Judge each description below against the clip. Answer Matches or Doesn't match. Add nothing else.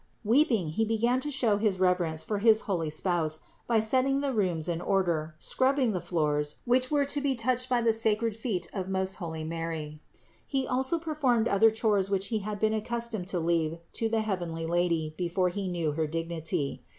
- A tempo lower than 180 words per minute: Doesn't match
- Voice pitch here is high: Matches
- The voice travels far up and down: Matches